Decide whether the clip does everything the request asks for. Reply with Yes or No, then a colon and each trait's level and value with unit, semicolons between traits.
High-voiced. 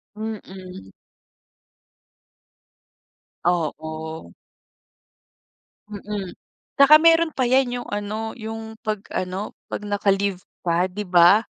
Yes: high, 205 Hz